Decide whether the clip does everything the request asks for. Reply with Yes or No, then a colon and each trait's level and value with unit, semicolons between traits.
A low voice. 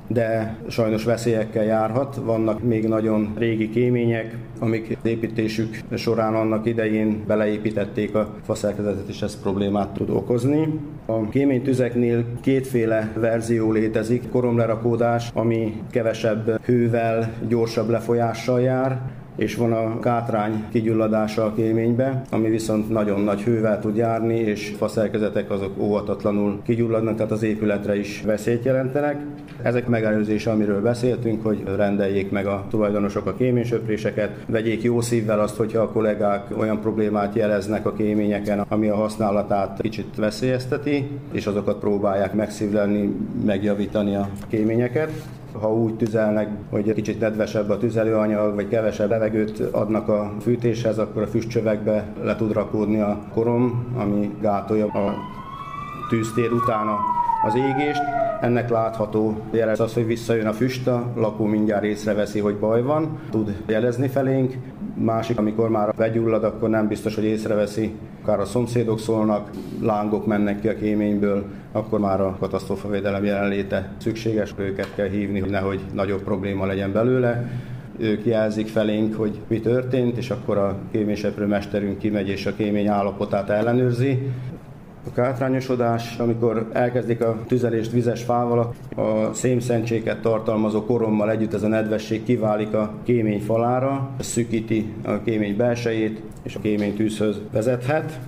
Yes: low, 110 Hz